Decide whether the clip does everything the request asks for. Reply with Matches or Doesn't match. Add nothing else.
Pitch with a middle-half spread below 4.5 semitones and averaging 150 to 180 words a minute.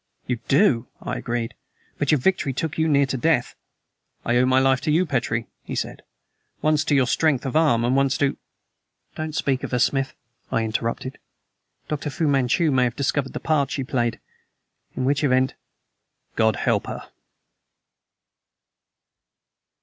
Matches